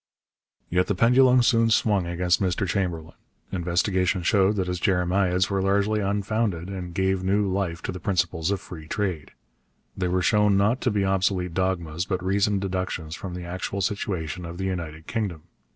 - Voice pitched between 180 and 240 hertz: No, very low, 95 Hz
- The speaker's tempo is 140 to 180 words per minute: Yes, average, 170 wpm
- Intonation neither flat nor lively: No, narrow, 2.1 semitones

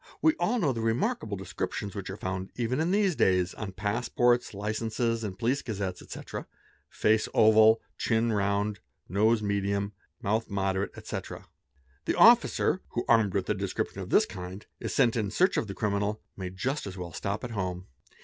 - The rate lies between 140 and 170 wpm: No, average, 180 wpm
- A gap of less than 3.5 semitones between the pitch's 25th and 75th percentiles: Yes, average, 3.1 semitones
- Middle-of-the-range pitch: No, low, 105 Hz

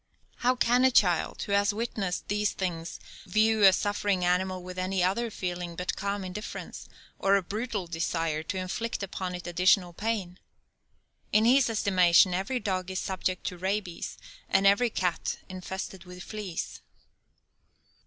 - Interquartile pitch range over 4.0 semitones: No, narrow, 2.5 semitones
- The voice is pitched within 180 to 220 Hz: Yes, high, 190 Hz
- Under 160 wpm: Yes, average, 150 wpm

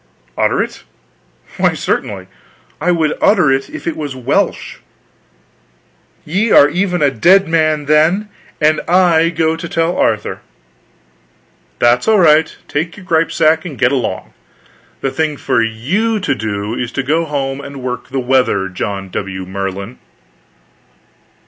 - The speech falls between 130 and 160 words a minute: Yes, average, 140 wpm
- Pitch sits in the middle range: Yes, medium, 150 Hz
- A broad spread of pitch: No, average, 5.0 semitones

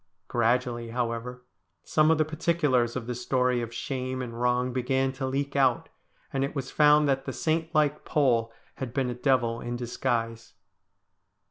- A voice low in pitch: Yes, low, 125 Hz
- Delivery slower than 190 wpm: Yes, average, 165 wpm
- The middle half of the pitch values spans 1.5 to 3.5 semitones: Yes, narrow, 2.5 semitones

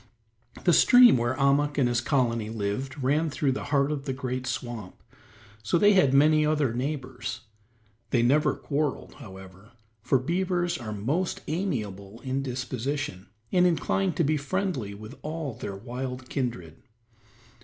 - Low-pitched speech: Yes, low, 130 Hz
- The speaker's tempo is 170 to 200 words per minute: No, average, 145 wpm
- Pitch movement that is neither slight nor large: Yes, average, 4.3 semitones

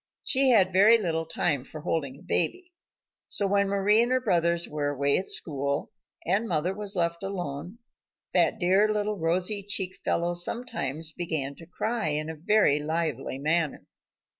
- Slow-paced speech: No, average, 165 wpm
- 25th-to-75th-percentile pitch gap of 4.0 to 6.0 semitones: Yes, average, 4.7 semitones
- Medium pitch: Yes, medium, 175 Hz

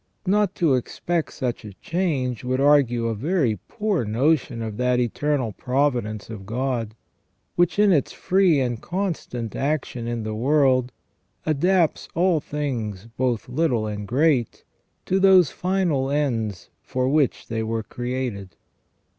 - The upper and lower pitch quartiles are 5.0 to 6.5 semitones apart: Yes, wide, 5.4 semitones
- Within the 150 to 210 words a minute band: No, average, 140 wpm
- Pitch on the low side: Yes, low, 130 Hz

